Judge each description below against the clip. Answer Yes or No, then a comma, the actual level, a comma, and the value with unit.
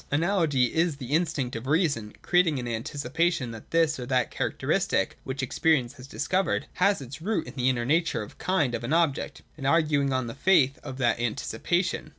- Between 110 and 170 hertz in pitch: Yes, medium, 140 Hz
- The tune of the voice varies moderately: Yes, average, 4.8 semitones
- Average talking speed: Yes, average, 190 wpm